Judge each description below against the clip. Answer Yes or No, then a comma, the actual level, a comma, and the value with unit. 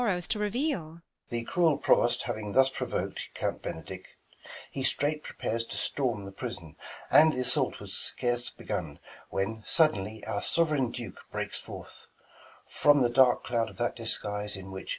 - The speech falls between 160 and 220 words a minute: No, average, 150 wpm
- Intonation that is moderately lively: No, wide, 5.8 semitones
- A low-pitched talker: Yes, low, 120 Hz